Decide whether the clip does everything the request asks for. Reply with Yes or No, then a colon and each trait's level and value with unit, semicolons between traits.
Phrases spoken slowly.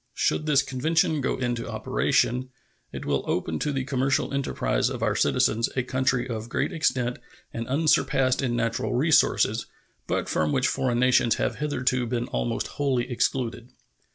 No: average, 155 wpm